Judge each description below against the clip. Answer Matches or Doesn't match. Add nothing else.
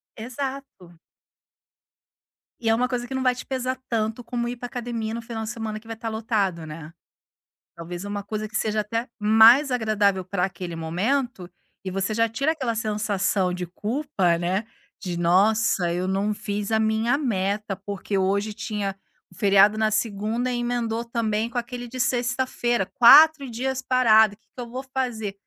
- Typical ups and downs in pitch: Matches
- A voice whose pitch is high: Matches